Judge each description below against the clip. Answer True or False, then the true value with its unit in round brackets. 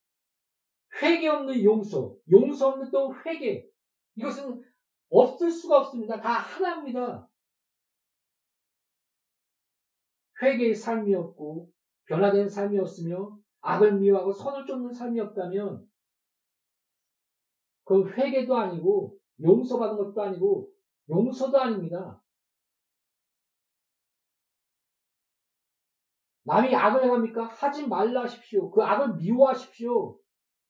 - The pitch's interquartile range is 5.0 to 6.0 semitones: True (5.5 semitones)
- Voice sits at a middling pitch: False (240 Hz)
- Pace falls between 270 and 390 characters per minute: False (210 characters per minute)